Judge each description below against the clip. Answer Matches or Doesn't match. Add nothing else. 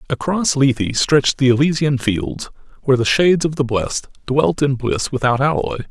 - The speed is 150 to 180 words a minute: Matches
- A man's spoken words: Matches